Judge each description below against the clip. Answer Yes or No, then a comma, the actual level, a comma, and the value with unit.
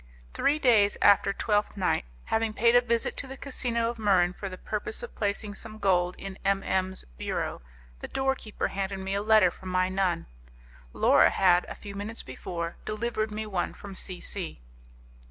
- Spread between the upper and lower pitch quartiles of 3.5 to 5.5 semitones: No, average, 2.9 semitones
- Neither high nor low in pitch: No, high, 200 Hz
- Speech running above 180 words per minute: Yes, average, 190 wpm